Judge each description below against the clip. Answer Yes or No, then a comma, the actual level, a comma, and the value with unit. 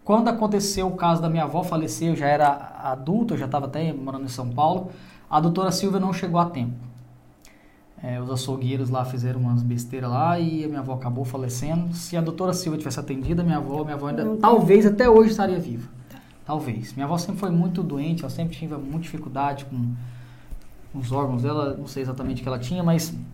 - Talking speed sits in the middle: No, fast, 210 wpm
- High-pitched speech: No, medium, 145 Hz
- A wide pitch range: No, average, 4.9 semitones